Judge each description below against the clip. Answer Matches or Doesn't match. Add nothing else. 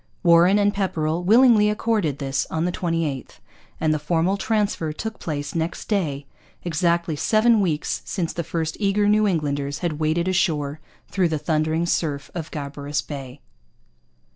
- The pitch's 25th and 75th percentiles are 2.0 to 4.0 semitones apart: Doesn't match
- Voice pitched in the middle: Matches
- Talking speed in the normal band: Matches